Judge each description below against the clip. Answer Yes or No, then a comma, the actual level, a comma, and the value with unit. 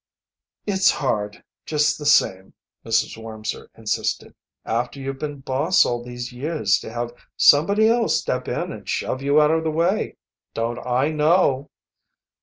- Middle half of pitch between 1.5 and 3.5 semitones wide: No, average, 4.6 semitones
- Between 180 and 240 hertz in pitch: No, low, 135 Hz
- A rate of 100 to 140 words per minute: No, average, 150 wpm